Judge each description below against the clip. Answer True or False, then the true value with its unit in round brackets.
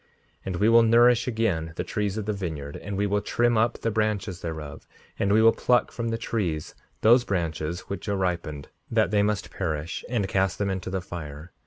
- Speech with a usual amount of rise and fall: True (4.5 semitones)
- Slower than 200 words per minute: False (205 wpm)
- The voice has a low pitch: True (100 Hz)